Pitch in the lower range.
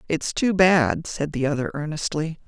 No: medium, 155 Hz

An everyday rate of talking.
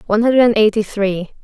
Yes: average, 165 wpm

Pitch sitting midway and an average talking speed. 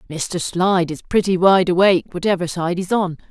Yes: medium, 180 Hz; average, 180 wpm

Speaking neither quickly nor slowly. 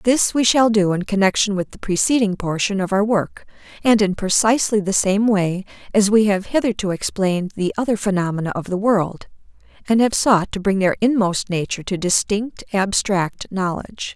Yes: average, 180 wpm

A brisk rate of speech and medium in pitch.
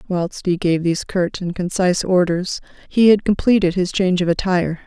No: average, 185 wpm; medium, 180 Hz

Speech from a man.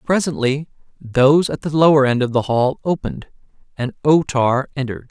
Yes: male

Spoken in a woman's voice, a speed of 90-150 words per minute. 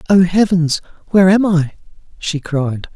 No: male; average, 140 wpm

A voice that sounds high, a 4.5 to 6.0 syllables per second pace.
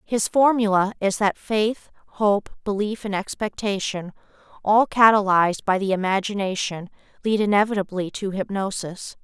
Yes: high, 200 Hz; 4.8 syllables/s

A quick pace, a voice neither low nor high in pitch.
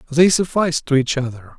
No: average, 190 wpm; medium, 145 Hz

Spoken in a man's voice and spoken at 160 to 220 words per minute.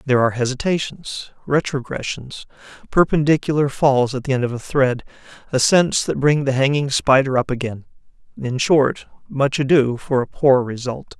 No: male; average, 150 wpm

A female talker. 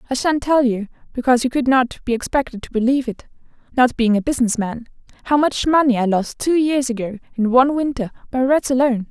Yes: female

